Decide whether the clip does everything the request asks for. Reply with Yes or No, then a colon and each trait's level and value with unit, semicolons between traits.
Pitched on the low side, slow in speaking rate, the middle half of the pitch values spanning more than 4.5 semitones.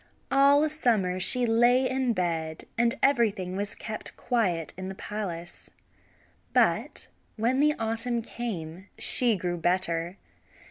No: high, 215 Hz; slow, 125 wpm; average, 5.1 semitones